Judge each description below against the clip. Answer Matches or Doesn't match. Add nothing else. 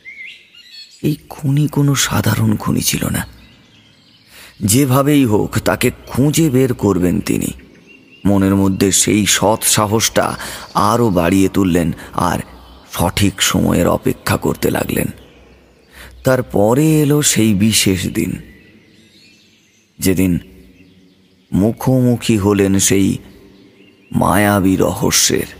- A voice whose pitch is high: Doesn't match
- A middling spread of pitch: Matches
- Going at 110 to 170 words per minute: Doesn't match